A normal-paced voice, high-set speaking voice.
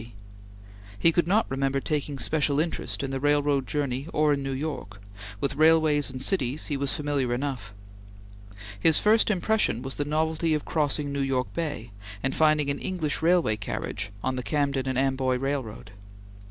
No: average, 165 wpm; medium, 140 Hz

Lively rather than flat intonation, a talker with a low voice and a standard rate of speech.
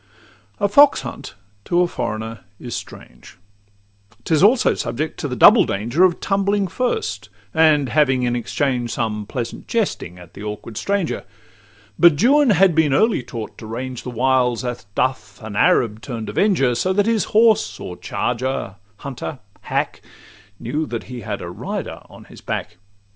Yes: wide, 7.8 semitones; low, 130 Hz; average, 160 wpm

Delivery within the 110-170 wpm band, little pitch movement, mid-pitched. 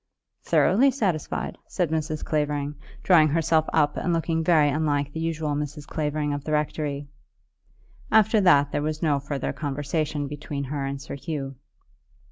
Yes: average, 150 wpm; narrow, 2.0 semitones; medium, 150 Hz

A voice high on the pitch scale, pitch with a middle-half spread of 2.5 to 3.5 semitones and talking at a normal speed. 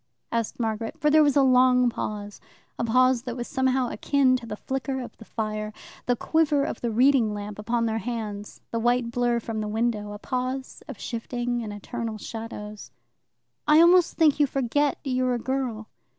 Yes: high, 240 Hz; average, 2.9 semitones; average, 185 wpm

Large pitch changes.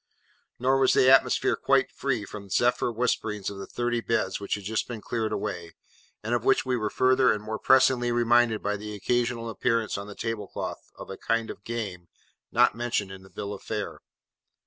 No: average, 2.8 semitones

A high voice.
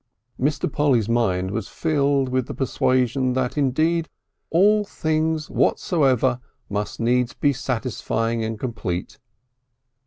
No: low, 130 Hz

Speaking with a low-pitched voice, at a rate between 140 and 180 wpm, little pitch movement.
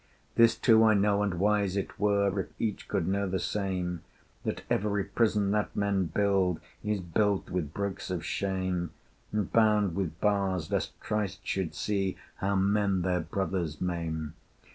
Yes: low, 100 Hz; average, 160 wpm; narrow, 2.1 semitones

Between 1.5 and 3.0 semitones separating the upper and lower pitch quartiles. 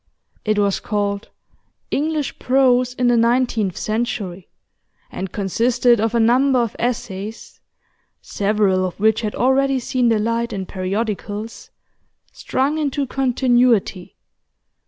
No: average, 3.5 semitones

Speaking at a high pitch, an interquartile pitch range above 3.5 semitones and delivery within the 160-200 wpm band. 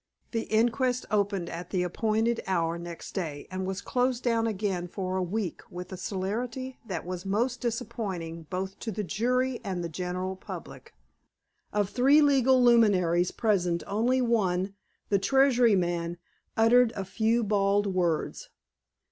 No: high, 200 Hz; average, 4.5 semitones; average, 150 wpm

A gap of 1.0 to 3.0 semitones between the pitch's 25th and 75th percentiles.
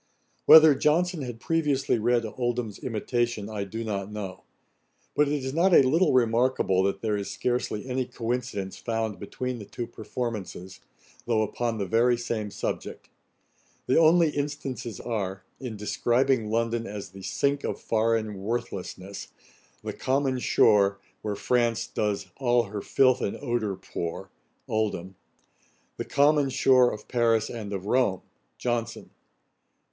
No: average, 3.7 semitones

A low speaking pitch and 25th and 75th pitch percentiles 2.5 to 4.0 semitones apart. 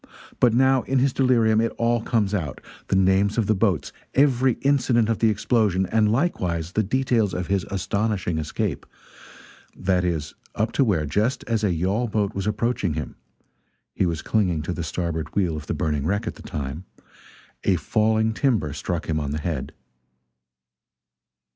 No: low, 100 Hz; average, 5.0 semitones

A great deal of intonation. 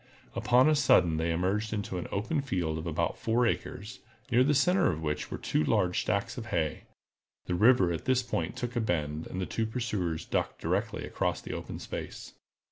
Yes: wide, 6.4 semitones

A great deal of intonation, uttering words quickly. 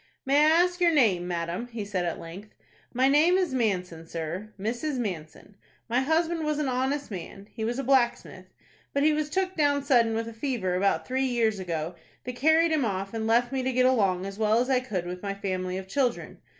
Yes: wide, 6.4 semitones; fast, 210 wpm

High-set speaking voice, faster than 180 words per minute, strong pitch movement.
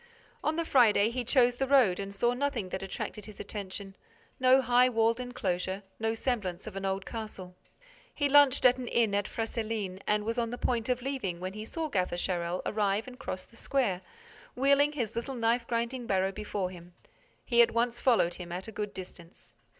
No: high, 225 Hz; average, 195 wpm; average, 4.4 semitones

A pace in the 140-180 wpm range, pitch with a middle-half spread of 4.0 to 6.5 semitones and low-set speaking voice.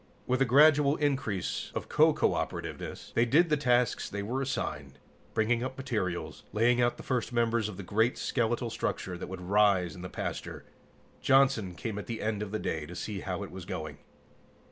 No: average, 190 wpm; average, 5.0 semitones; low, 110 Hz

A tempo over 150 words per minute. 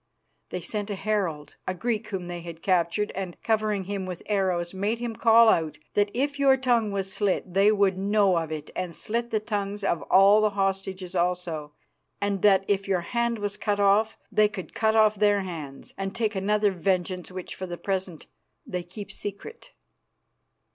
Yes: average, 185 wpm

